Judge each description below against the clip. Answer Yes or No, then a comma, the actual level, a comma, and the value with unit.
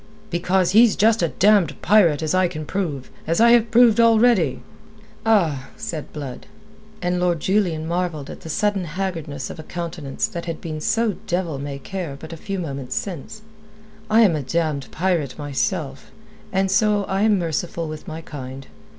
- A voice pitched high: No, medium, 170 Hz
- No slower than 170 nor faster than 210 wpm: Yes, average, 175 wpm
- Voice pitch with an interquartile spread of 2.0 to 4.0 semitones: No, average, 4.6 semitones